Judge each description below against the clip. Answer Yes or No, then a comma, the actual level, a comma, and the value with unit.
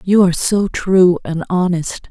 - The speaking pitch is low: No, medium, 180 Hz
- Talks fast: No, average, 170 wpm